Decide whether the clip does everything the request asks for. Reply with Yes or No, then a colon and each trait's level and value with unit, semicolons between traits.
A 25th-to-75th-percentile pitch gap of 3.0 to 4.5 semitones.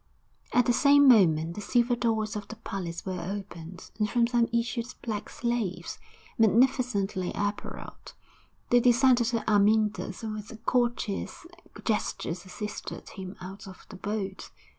Yes: average, 3.6 semitones